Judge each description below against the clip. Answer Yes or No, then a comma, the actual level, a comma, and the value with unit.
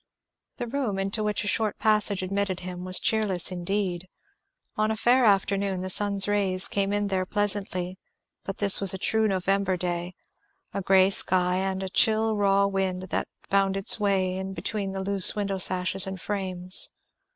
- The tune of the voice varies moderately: No, narrow, 1.7 semitones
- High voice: Yes, high, 195 Hz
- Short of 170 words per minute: No, average, 175 wpm